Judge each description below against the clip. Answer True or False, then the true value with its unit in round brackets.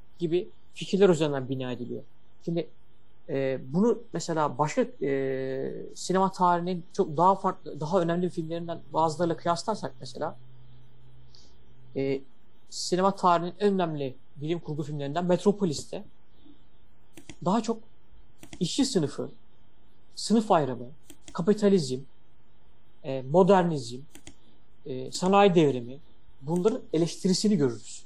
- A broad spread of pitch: True (5.9 semitones)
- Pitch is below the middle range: False (165 Hz)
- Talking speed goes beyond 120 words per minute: False (100 wpm)